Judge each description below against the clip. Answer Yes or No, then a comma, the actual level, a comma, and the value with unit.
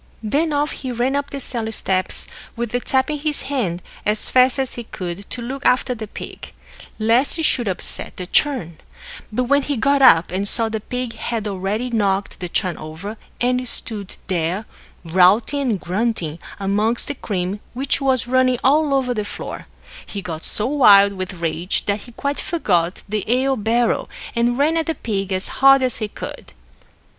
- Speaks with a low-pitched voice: No, high, 230 Hz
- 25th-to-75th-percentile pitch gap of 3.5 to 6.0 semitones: Yes, average, 5.1 semitones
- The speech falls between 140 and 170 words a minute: No, average, 185 wpm